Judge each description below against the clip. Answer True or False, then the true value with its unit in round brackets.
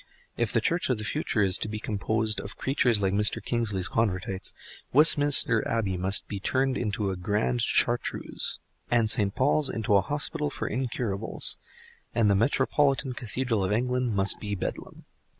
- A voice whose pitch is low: True (110 Hz)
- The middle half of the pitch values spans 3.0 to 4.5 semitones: True (4.1 semitones)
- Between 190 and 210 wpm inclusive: False (165 wpm)